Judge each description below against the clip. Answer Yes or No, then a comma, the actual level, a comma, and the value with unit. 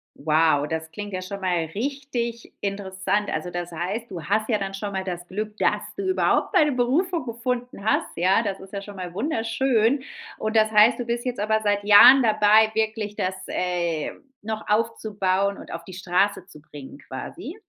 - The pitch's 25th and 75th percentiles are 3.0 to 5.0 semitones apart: Yes, average, 3.6 semitones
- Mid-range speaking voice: No, high, 205 Hz